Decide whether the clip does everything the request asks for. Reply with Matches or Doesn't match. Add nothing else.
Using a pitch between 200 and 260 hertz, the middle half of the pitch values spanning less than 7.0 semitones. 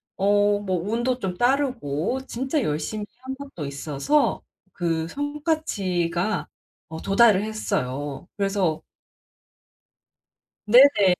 Doesn't match